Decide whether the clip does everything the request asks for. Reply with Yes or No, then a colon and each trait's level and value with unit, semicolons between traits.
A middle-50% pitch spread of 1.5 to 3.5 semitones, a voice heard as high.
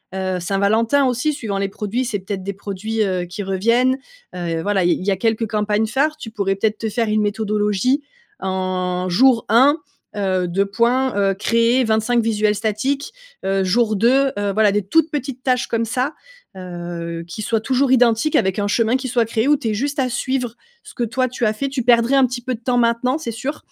No: average, 4.1 semitones; high, 220 Hz